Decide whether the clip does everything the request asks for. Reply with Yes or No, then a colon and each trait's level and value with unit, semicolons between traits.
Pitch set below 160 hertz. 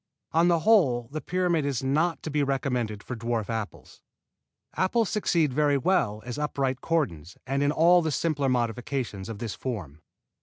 Yes: medium, 140 Hz